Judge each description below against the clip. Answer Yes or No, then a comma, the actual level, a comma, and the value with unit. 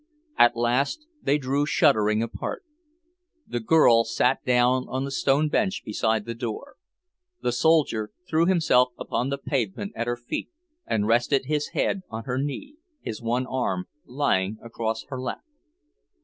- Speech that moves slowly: No, average, 150 wpm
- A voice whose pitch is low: Yes, low, 125 Hz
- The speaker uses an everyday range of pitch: Yes, average, 3.7 semitones